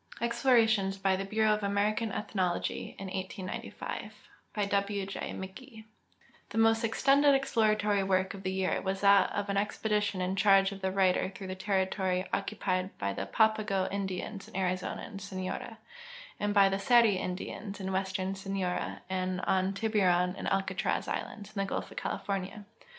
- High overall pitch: Yes, high, 195 Hz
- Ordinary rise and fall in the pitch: No, narrow, 1.9 semitones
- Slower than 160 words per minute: No, average, 165 wpm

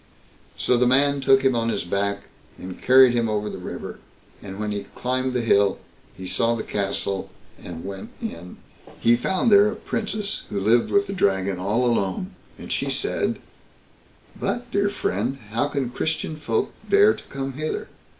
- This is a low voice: Yes, low, 120 Hz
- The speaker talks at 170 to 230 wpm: Yes, average, 175 wpm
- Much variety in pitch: Yes, wide, 6.4 semitones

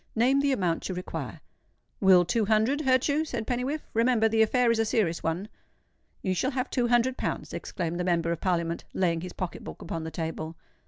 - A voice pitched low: No, high, 215 Hz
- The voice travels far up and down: Yes, wide, 6.4 semitones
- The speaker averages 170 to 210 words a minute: Yes, average, 200 wpm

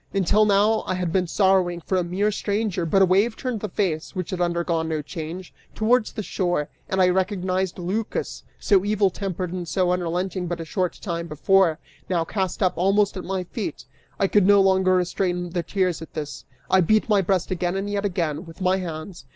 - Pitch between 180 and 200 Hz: Yes, medium, 185 Hz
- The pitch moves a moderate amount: No, narrow, 2.3 semitones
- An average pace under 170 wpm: No, fast, 205 wpm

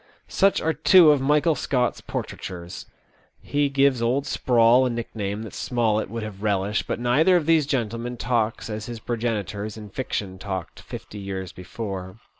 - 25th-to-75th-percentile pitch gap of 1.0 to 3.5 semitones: No, average, 4.3 semitones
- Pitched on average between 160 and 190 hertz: No, low, 115 Hz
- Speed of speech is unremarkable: Yes, average, 160 wpm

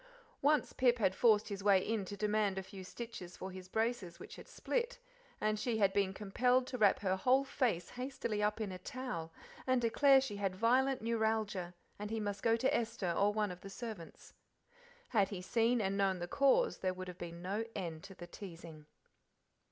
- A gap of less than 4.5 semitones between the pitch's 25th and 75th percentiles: Yes, average, 4.0 semitones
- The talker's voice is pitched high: Yes, high, 210 Hz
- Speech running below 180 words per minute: No, average, 200 wpm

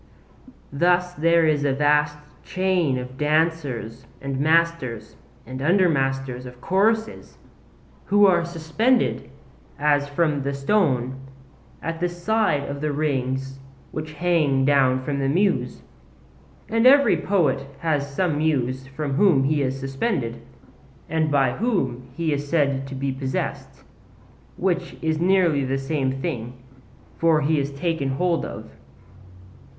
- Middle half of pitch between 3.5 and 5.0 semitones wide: Yes, average, 4.0 semitones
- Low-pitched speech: No, medium, 150 Hz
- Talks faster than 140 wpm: No, slow, 135 wpm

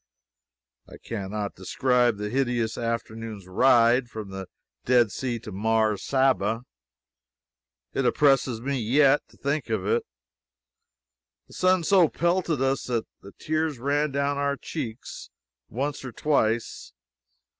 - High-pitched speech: No, low, 125 Hz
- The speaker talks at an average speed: No, slow, 130 wpm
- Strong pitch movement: No, average, 4.1 semitones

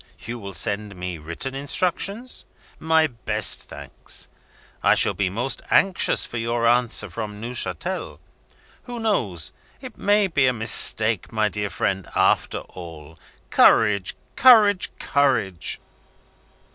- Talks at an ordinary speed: No, slow, 120 wpm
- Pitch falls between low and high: No, low, 115 Hz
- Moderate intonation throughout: No, wide, 6.7 semitones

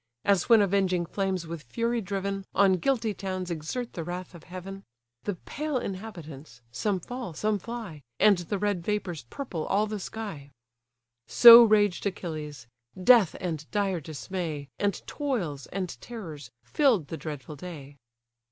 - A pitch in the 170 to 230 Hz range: Yes, medium, 185 Hz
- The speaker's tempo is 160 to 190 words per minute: No, average, 145 wpm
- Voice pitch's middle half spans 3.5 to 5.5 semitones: Yes, average, 4.6 semitones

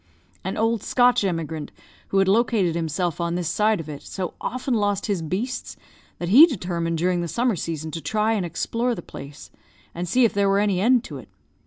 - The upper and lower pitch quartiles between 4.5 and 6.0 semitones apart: Yes, average, 5.0 semitones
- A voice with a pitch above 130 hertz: Yes, high, 190 Hz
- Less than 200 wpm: No, fast, 205 wpm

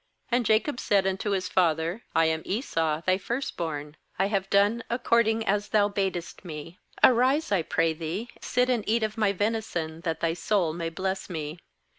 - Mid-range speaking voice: No, high, 195 Hz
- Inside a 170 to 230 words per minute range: Yes, average, 180 wpm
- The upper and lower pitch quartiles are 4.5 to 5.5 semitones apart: Yes, average, 4.9 semitones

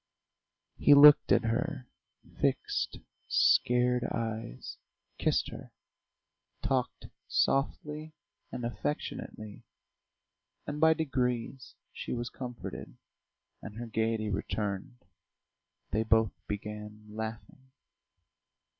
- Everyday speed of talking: No, slow, 85 wpm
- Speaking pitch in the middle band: No, low, 120 Hz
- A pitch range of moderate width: Yes, average, 3.4 semitones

